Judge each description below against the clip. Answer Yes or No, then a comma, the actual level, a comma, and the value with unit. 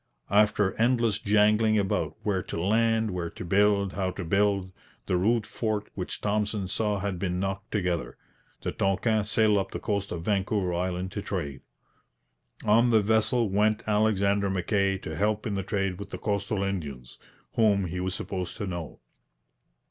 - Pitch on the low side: Yes, low, 100 Hz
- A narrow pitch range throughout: Yes, narrow, 2.2 semitones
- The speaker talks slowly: No, average, 165 wpm